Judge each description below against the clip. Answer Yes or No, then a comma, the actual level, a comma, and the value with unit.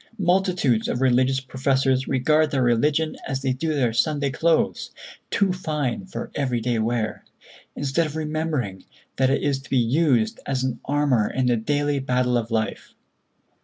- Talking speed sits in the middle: Yes, average, 160 wpm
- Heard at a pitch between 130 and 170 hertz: Yes, low, 135 Hz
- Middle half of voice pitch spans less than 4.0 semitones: Yes, average, 3.6 semitones